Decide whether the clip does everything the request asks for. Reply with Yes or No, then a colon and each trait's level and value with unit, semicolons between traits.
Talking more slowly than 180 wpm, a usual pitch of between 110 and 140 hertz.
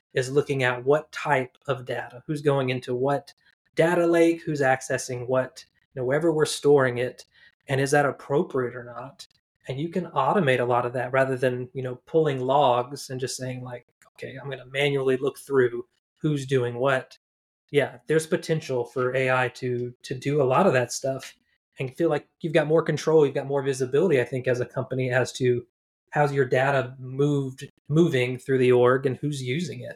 No: average, 200 wpm; low, 135 Hz